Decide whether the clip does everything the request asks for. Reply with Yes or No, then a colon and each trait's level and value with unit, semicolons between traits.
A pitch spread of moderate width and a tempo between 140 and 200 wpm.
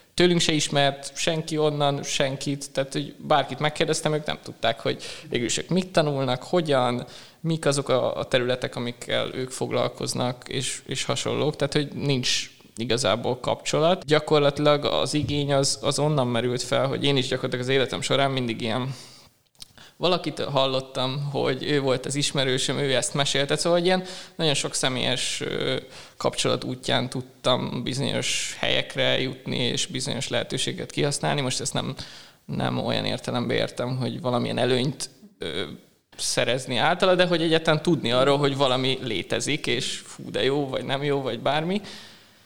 Yes: average, 3.0 semitones; average, 145 wpm